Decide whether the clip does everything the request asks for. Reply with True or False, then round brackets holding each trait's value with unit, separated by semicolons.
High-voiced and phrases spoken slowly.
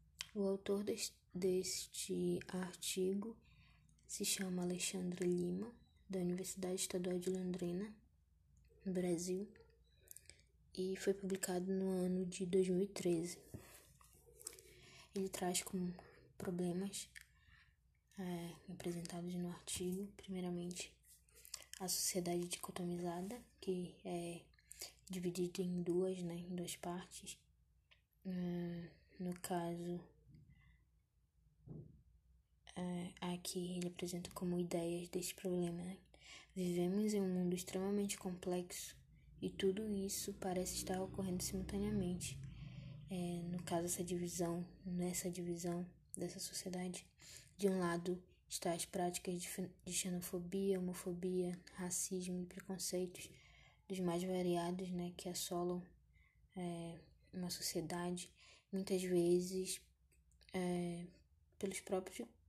False (180 Hz; 95 wpm)